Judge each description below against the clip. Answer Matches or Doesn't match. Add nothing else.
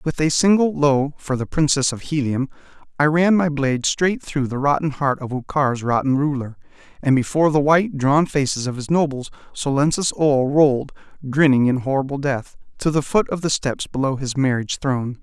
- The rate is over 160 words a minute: Matches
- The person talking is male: Matches